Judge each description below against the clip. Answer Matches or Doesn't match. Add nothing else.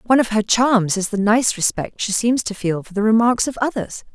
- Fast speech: Matches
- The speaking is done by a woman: Matches